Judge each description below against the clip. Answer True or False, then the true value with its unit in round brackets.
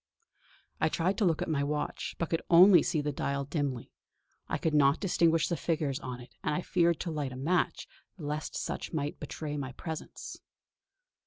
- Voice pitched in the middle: True (155 Hz)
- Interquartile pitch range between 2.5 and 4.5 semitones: True (2.9 semitones)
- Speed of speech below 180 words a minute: False (185 wpm)